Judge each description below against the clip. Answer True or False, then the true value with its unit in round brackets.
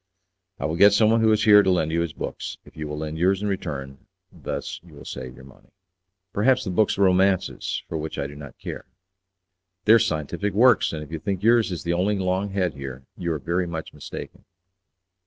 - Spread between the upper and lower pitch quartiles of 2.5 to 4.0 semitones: False (4.8 semitones)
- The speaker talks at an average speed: False (220 wpm)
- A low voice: True (90 Hz)